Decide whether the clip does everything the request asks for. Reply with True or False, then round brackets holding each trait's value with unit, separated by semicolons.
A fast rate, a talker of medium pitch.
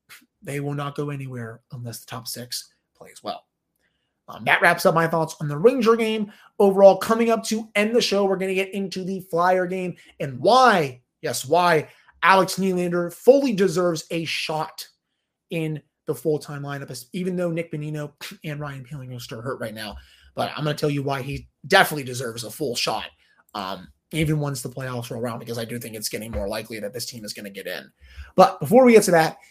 True (215 wpm; 155 Hz)